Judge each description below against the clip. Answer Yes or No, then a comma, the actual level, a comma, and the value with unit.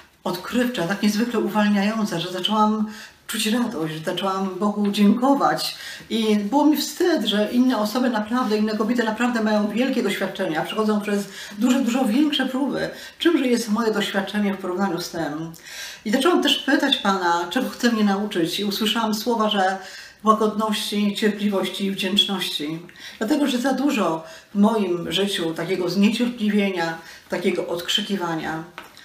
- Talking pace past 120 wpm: Yes, average, 140 wpm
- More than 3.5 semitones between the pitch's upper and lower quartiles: Yes, average, 3.9 semitones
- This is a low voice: No, high, 210 Hz